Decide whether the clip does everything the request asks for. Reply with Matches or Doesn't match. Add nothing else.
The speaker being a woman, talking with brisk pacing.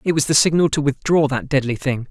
Doesn't match